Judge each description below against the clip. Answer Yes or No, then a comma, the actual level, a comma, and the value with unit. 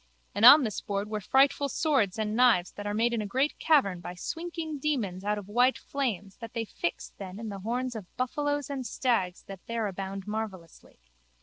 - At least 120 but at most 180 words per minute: No, average, 200 wpm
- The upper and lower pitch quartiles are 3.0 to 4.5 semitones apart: No, average, 4.9 semitones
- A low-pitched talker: No, high, 220 Hz